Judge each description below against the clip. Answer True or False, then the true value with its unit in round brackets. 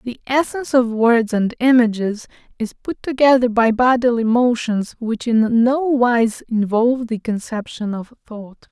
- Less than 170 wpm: True (145 wpm)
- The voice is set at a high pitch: True (235 Hz)